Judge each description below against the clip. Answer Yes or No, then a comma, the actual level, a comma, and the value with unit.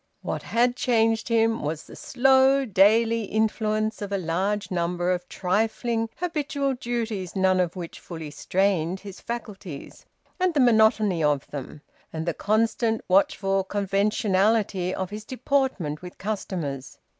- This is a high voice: Yes, high, 205 Hz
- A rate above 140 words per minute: No, slow, 135 wpm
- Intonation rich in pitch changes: No, average, 3.8 semitones